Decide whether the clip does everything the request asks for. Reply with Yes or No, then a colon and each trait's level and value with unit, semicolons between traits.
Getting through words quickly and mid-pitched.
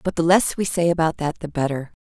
Yes: fast, 265 wpm; medium, 165 Hz